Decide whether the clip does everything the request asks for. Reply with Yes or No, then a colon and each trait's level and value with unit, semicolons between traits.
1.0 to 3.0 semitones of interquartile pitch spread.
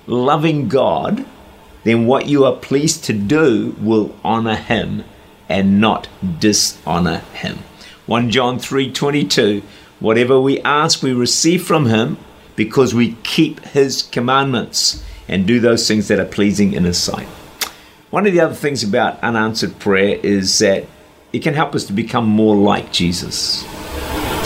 No: average, 4.9 semitones